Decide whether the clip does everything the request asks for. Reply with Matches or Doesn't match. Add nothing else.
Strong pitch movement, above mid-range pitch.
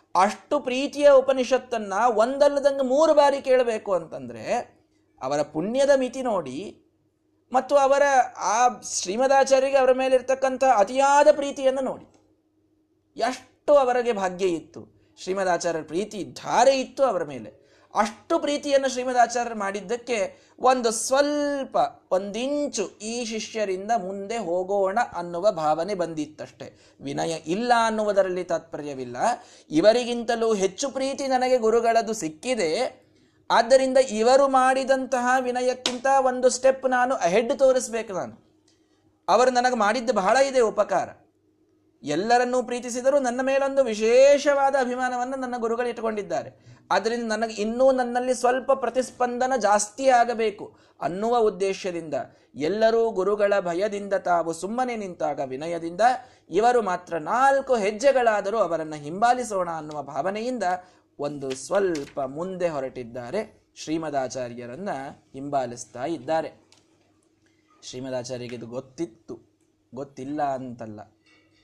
Matches